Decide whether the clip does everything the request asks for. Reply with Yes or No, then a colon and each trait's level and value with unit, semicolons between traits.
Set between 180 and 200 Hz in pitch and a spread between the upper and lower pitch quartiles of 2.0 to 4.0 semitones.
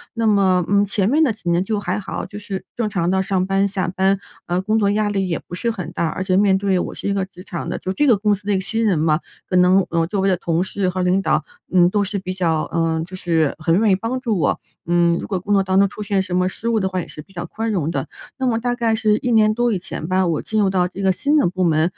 Yes: high, 190 Hz; narrow, 2.6 semitones